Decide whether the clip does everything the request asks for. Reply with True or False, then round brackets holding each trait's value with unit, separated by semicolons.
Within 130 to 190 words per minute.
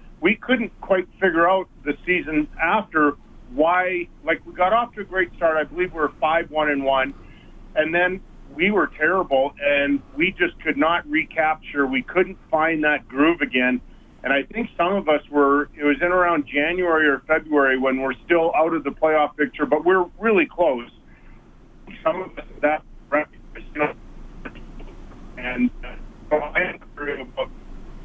True (160 wpm)